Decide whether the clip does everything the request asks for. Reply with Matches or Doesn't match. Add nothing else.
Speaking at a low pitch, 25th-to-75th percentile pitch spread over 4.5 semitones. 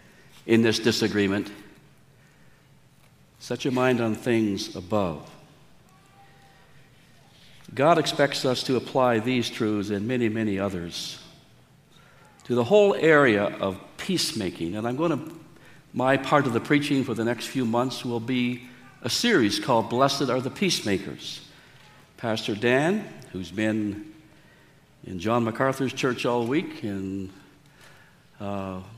Doesn't match